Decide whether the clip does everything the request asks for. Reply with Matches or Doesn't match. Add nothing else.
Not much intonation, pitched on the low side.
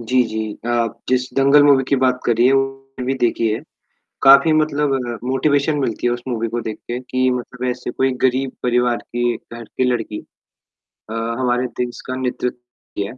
Matches